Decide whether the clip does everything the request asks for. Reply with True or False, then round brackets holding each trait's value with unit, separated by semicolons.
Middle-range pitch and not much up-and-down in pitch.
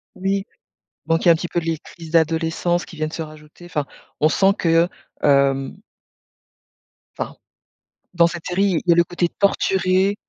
True (170 Hz; 2.3 semitones)